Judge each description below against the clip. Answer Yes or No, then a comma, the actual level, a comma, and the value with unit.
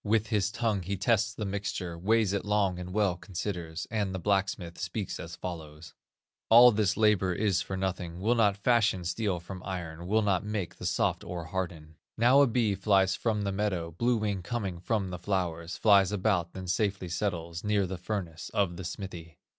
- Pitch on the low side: Yes, very low, 95 Hz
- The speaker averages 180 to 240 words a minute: Yes, average, 190 wpm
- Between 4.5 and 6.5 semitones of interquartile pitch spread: No, average, 3.1 semitones